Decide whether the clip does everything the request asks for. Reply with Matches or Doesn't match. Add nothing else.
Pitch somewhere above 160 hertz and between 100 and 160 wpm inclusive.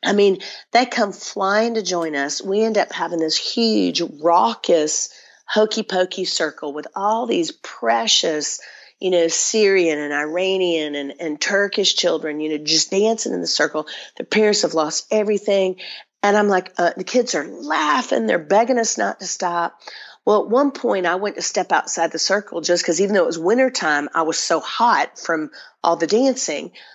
Doesn't match